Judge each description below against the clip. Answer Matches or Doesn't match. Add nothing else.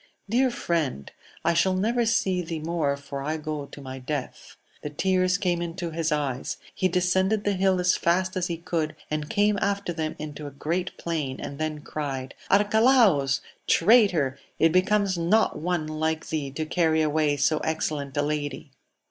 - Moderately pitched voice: Matches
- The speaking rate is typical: Matches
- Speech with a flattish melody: Doesn't match